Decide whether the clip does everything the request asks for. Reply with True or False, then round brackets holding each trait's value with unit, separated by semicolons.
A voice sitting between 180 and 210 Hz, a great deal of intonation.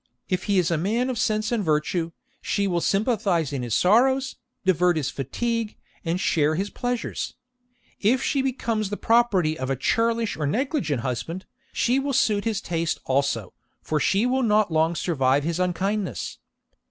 True (190 Hz; 6.4 semitones)